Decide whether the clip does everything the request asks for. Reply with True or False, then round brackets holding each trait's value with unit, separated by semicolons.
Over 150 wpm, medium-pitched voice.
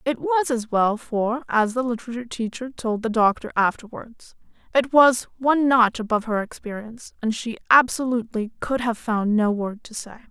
False (175 wpm; 235 Hz)